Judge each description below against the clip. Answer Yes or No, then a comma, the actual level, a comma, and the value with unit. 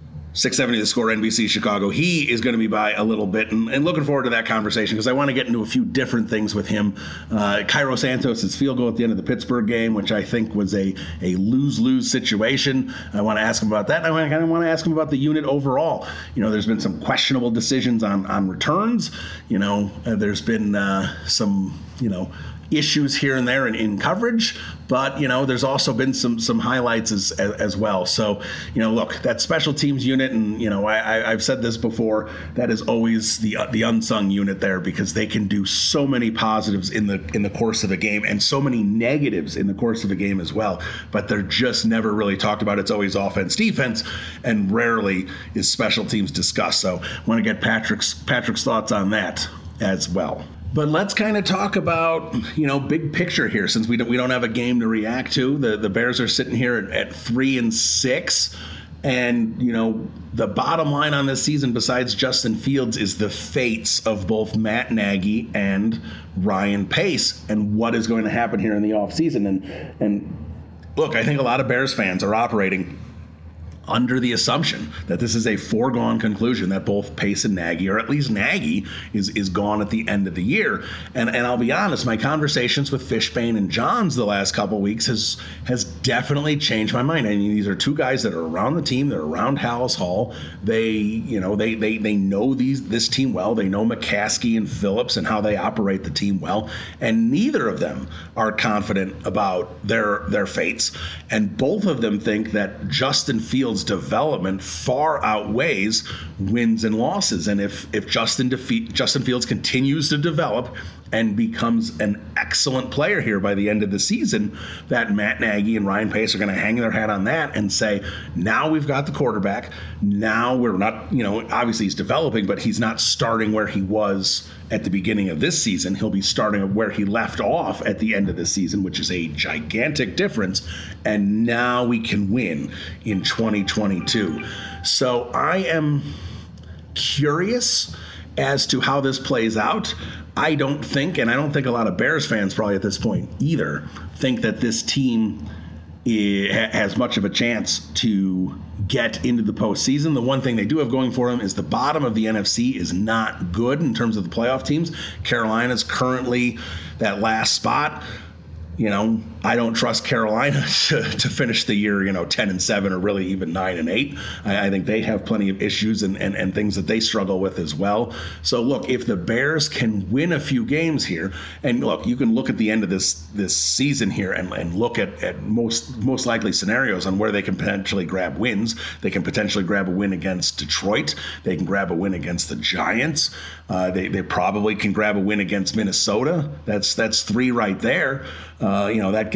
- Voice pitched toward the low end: Yes, low, 110 Hz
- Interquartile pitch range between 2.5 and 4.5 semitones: Yes, average, 3.9 semitones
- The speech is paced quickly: Yes, fast, 210 wpm